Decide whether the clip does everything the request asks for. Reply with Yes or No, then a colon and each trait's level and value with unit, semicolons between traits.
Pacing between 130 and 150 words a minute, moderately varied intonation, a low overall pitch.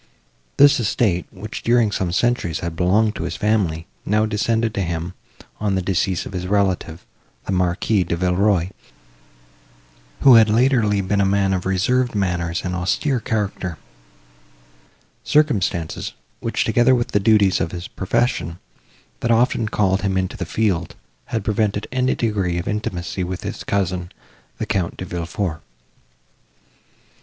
Yes: average, 145 wpm; average, 3.6 semitones; low, 100 Hz